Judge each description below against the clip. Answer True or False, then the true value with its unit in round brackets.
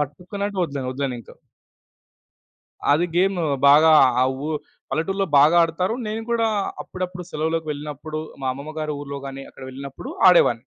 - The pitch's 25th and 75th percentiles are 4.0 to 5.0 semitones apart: True (4.4 semitones)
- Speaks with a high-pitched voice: False (155 Hz)